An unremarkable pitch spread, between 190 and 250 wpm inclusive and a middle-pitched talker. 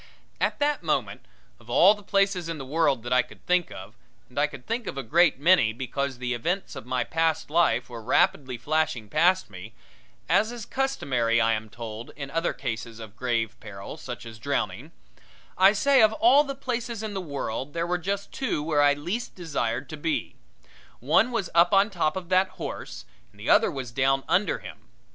No: wide, 7.6 semitones; average, 200 wpm; medium, 150 Hz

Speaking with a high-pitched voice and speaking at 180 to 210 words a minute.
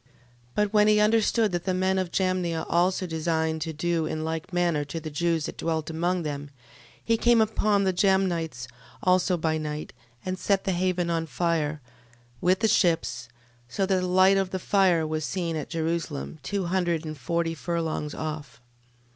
No: medium, 170 Hz; average, 185 wpm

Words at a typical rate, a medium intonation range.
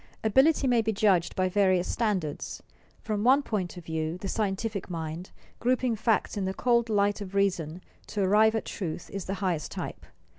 Yes: average, 185 wpm; average, 3.4 semitones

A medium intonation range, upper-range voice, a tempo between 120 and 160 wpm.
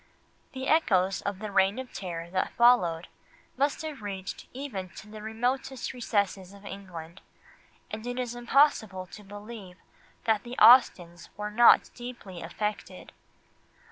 Yes: average, 4.4 semitones; high, 210 Hz; average, 140 wpm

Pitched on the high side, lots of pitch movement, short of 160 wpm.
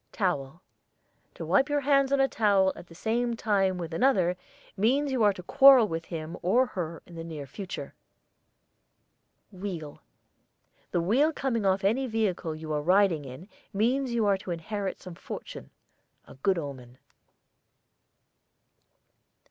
Yes: high, 195 Hz; wide, 6.0 semitones; average, 150 wpm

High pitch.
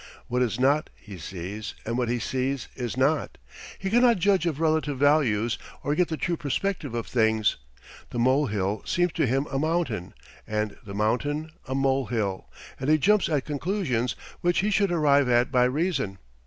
No: low, 135 Hz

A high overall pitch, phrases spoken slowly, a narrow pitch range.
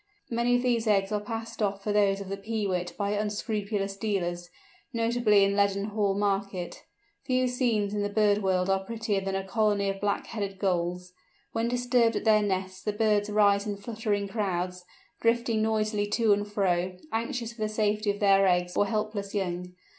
No: high, 205 Hz; average, 180 wpm; narrow, 2.0 semitones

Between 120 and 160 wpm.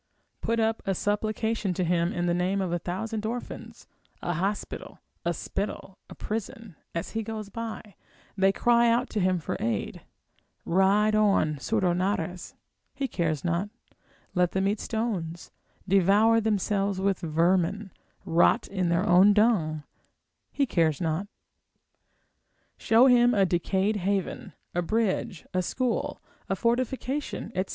Yes: average, 140 wpm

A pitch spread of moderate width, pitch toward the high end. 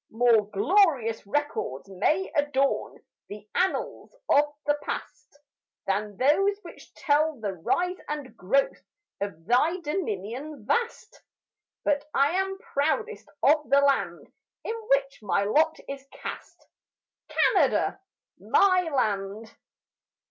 No: wide, 7.0 semitones; very high, 280 Hz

